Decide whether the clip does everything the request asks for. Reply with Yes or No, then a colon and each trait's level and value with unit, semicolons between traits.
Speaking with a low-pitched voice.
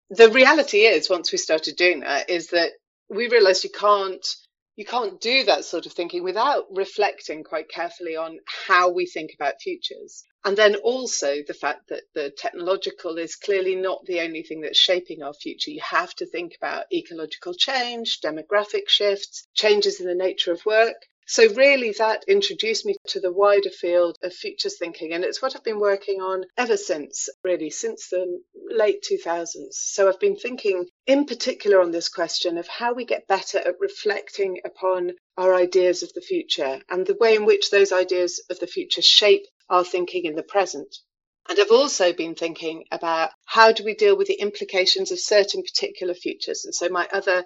No: high, 200 Hz